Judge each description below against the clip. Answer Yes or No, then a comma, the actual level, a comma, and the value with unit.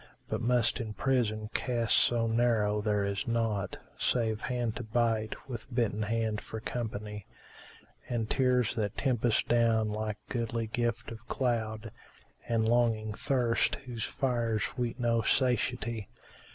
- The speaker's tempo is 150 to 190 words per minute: No, average, 140 wpm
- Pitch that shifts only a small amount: Yes, narrow, 1.9 semitones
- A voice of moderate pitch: No, low, 115 Hz